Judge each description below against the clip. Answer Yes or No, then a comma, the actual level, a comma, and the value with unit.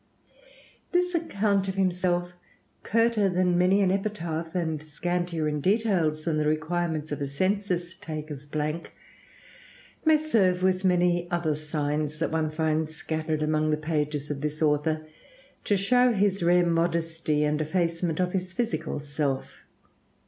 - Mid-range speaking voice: Yes, medium, 170 Hz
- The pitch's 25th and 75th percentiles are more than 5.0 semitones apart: No, average, 3.3 semitones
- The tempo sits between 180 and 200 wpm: No, average, 140 wpm